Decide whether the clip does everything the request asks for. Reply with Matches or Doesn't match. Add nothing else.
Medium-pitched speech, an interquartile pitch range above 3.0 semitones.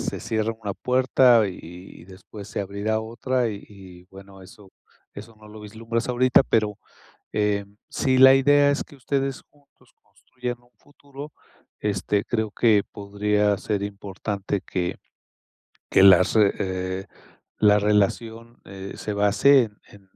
Doesn't match